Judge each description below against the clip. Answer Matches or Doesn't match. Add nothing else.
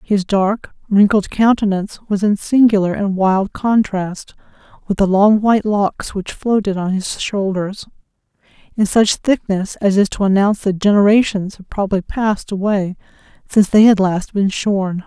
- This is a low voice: Doesn't match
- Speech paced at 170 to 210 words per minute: Doesn't match